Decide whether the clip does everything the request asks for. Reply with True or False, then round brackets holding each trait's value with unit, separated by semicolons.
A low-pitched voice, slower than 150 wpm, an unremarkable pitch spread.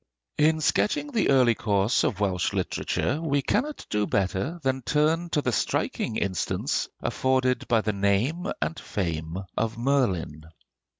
False (125 Hz; 140 wpm; 7.2 semitones)